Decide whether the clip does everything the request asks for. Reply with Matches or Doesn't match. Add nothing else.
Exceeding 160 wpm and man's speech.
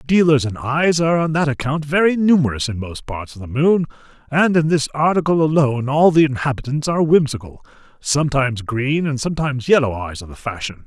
Matches